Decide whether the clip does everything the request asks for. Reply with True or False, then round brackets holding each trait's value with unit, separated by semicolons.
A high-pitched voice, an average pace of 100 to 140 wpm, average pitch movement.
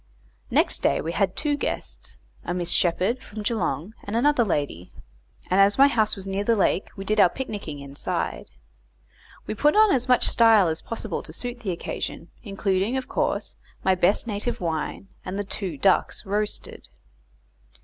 False (200 Hz; 170 wpm; 4.3 semitones)